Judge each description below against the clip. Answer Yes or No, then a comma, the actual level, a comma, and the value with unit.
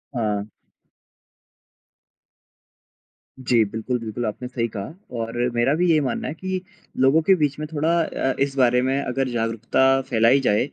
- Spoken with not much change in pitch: No, average, 3.3 semitones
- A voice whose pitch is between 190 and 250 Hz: No, low, 130 Hz